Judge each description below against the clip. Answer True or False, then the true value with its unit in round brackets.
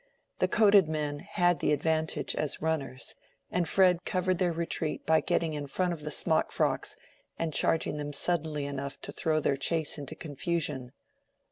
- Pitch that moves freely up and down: False (2.9 semitones)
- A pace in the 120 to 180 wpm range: True (165 wpm)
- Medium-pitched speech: True (160 Hz)